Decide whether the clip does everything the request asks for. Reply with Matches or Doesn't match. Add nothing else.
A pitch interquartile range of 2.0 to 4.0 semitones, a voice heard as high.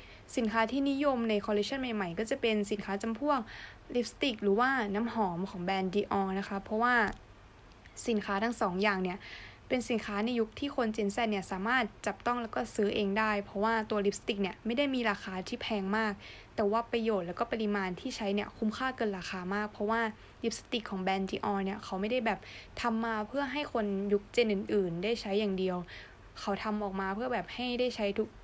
Matches